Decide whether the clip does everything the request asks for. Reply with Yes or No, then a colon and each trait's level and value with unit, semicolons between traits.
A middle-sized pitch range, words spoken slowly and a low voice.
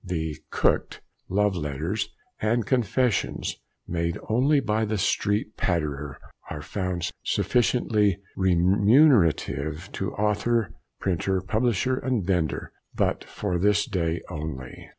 Yes: average, 4.6 semitones; slow, 110 wpm; very low, 95 Hz